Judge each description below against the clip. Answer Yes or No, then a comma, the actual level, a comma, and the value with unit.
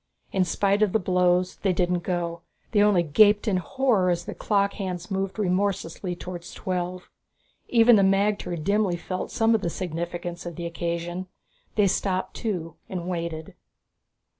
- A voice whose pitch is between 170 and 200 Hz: Yes, medium, 185 Hz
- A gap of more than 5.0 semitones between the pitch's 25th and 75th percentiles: No, narrow, 2.5 semitones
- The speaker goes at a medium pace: Yes, average, 160 wpm